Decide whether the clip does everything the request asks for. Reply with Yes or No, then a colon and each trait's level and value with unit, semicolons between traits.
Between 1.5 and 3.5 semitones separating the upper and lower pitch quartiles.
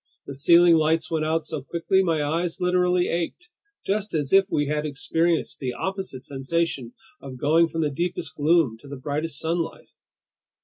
Yes: average, 3.1 semitones